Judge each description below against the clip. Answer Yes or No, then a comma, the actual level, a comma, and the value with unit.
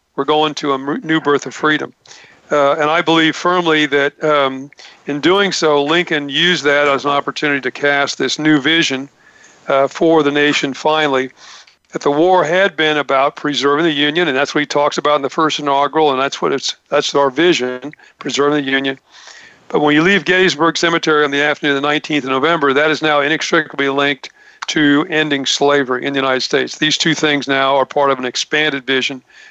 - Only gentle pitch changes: Yes, narrow, 1.9 semitones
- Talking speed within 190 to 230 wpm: Yes, average, 200 wpm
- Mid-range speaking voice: Yes, medium, 145 Hz